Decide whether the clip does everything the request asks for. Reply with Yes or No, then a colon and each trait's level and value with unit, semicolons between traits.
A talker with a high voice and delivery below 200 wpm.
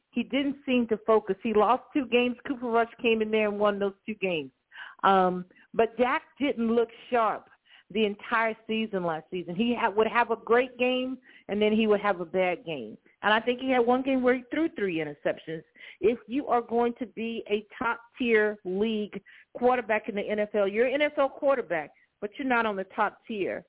No: high, 225 Hz; fast, 205 wpm